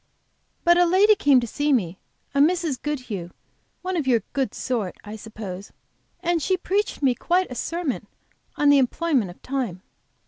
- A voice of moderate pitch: No, very high, 275 Hz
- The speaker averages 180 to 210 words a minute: No, average, 170 wpm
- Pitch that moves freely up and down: Yes, wide, 7.4 semitones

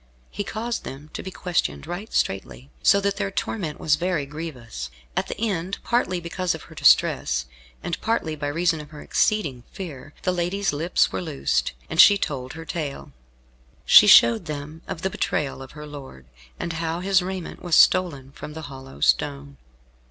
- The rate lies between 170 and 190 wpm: Yes, average, 180 wpm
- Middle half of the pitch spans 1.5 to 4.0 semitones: No, average, 4.6 semitones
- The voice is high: No, medium, 160 Hz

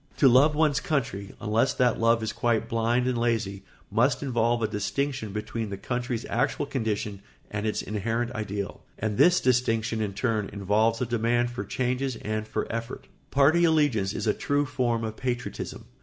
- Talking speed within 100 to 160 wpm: No, average, 170 wpm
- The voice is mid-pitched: No, low, 115 Hz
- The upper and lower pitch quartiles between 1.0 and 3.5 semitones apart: Yes, average, 2.9 semitones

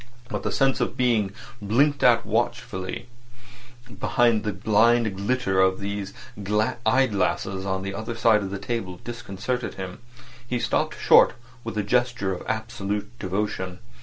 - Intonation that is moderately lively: Yes, average, 3.5 semitones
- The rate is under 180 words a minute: Yes, average, 145 wpm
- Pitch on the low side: Yes, low, 105 Hz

